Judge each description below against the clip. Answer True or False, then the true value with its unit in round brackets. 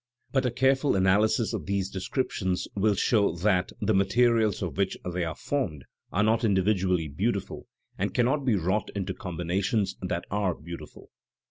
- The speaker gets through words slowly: False (155 wpm)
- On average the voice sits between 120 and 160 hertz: False (100 Hz)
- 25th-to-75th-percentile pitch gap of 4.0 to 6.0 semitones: False (3.6 semitones)